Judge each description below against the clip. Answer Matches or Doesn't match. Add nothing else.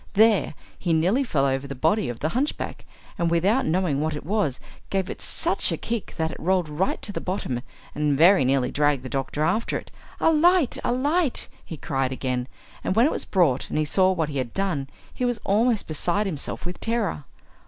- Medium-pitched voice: Matches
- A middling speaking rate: Doesn't match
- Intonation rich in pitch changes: Matches